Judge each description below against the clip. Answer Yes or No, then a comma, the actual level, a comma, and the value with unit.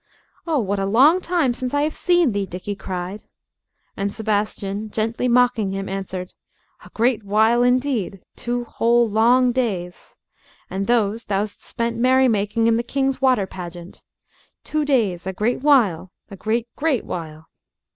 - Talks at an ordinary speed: Yes, average, 150 wpm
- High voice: Yes, high, 225 Hz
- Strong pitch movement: No, average, 4.2 semitones